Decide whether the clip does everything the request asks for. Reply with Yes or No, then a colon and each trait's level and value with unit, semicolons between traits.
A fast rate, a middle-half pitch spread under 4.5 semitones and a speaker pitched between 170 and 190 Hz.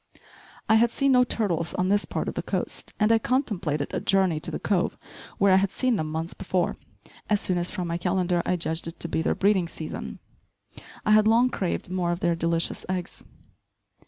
Yes: fast, 210 wpm; average, 3.8 semitones; medium, 185 Hz